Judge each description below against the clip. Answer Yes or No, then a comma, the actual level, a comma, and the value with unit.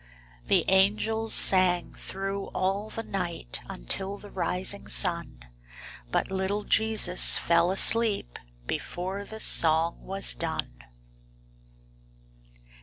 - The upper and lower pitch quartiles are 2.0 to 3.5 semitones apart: Yes, narrow, 2.5 semitones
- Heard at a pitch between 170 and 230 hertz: Yes, high, 190 Hz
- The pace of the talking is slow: Yes, slow, 100 wpm